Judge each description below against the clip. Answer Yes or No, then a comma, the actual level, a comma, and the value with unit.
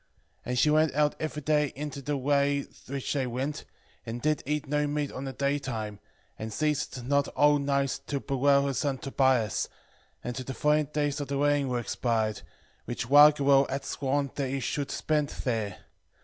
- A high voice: No, medium, 140 Hz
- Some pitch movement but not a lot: No, narrow, 2.2 semitones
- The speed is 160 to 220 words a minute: Yes, average, 175 wpm